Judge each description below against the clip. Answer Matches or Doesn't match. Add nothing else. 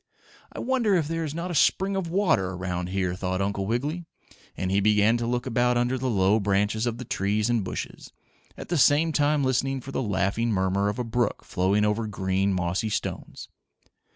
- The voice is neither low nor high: Doesn't match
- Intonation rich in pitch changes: Matches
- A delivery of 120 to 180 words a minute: Doesn't match